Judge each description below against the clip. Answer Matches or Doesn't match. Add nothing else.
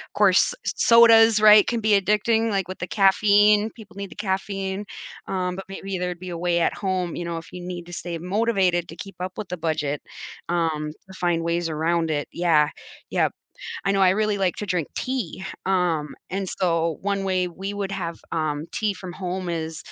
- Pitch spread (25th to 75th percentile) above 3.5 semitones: Doesn't match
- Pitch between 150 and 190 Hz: Matches